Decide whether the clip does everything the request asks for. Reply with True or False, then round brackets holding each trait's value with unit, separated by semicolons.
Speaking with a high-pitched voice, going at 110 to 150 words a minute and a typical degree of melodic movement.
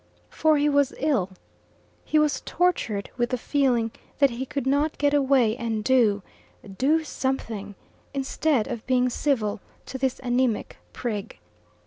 True (260 Hz; 140 wpm; 3.8 semitones)